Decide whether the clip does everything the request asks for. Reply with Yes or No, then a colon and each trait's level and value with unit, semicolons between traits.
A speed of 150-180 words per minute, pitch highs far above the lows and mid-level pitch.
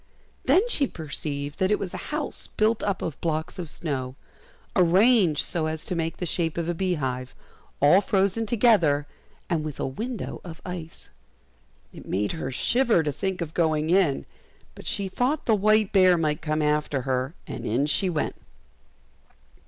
No: average, 170 wpm; average, 4.9 semitones; medium, 170 Hz